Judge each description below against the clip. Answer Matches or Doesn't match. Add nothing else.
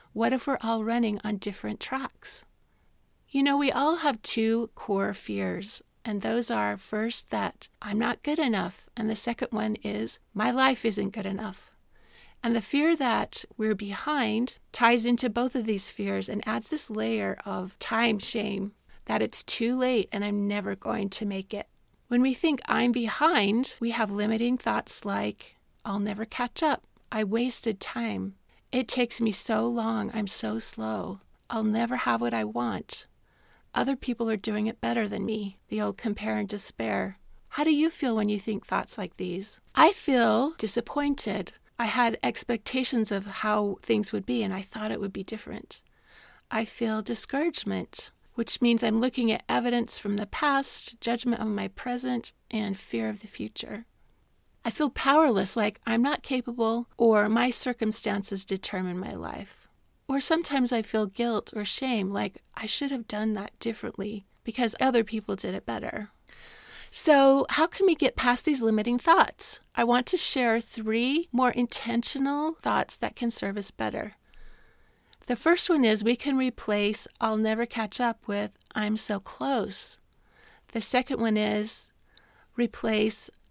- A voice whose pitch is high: Matches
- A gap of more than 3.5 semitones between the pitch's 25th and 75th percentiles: Doesn't match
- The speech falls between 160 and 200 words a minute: Matches